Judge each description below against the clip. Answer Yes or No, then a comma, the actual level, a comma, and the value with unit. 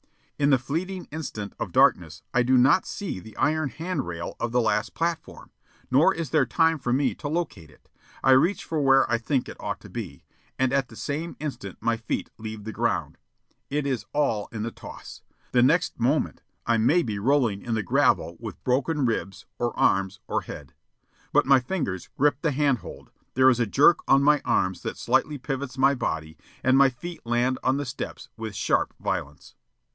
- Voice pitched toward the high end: No, low, 130 Hz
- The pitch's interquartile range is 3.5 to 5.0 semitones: Yes, average, 4.5 semitones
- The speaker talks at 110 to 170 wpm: No, average, 200 wpm